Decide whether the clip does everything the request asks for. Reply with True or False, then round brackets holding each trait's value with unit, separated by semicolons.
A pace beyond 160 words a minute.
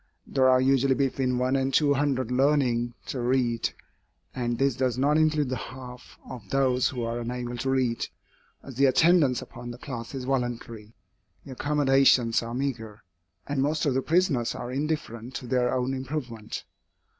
True (170 wpm)